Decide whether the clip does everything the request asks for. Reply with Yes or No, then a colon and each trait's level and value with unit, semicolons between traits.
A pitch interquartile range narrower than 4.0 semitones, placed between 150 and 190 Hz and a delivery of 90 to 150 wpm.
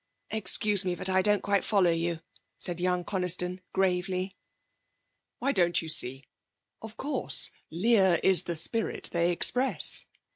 Yes: average, 2.7 semitones; medium, 185 Hz; average, 140 wpm